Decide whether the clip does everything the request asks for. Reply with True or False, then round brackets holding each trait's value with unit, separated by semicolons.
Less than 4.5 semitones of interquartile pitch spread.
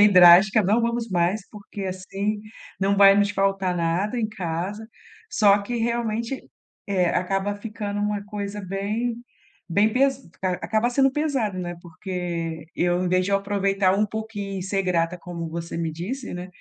True (2.9 semitones)